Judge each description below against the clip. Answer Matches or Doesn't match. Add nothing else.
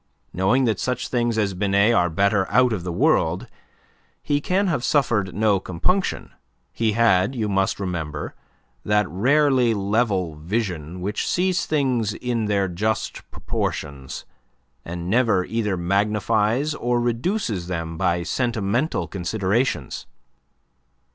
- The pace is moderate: Doesn't match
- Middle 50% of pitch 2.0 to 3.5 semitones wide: Doesn't match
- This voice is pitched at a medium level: Doesn't match